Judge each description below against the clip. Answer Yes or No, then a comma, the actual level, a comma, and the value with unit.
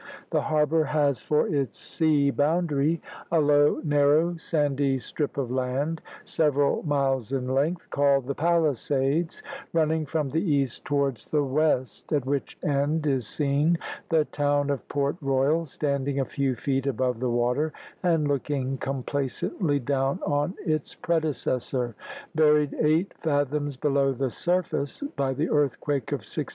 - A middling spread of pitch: No, narrow, 2.3 semitones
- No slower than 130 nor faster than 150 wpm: Yes, average, 140 wpm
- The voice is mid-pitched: Yes, medium, 145 Hz